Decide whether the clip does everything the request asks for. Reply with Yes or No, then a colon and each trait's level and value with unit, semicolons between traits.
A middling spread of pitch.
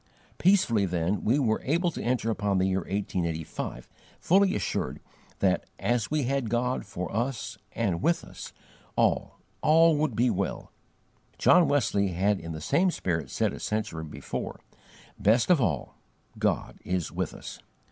No: wide, 7.0 semitones